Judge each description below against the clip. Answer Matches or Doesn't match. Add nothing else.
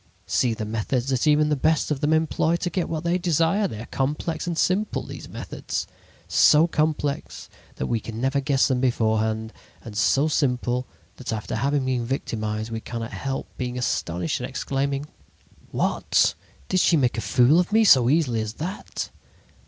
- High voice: Doesn't match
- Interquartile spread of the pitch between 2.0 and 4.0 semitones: Doesn't match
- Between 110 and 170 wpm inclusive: Doesn't match